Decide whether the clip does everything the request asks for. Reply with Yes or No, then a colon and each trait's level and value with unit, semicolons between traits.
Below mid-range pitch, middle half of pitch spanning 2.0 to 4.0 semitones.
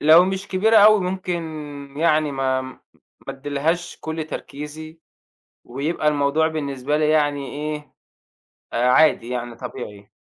No: medium, 150 Hz; average, 3.0 semitones